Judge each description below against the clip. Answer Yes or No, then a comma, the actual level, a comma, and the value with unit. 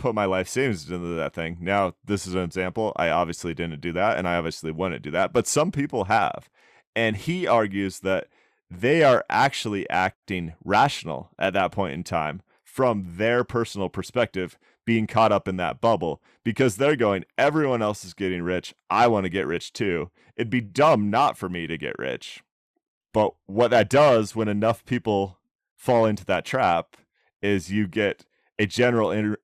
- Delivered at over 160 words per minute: Yes, average, 185 wpm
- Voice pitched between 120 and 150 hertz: No, low, 100 Hz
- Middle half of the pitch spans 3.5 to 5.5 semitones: Yes, average, 4.2 semitones